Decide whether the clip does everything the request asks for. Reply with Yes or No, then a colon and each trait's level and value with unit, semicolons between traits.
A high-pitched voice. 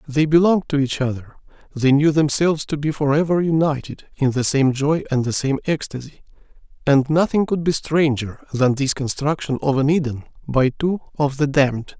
No: medium, 145 Hz